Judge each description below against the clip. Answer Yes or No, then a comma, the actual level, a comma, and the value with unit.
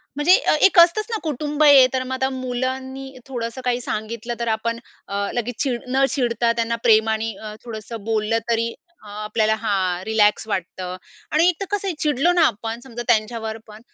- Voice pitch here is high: Yes, high, 235 Hz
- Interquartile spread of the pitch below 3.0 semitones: No, average, 3.4 semitones